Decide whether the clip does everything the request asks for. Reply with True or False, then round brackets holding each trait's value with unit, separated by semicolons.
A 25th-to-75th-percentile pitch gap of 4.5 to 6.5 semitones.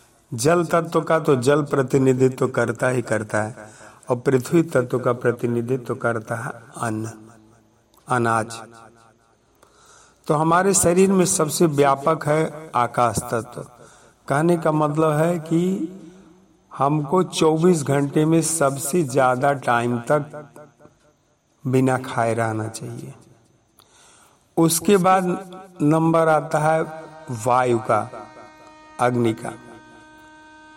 True (5.3 semitones)